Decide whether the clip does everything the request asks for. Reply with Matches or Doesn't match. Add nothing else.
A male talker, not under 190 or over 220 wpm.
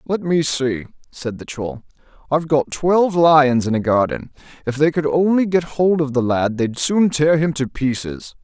Matches